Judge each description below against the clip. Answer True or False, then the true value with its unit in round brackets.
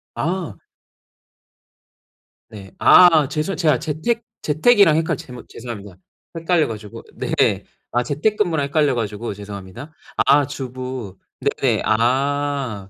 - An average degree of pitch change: False (5.7 semitones)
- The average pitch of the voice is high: False (140 Hz)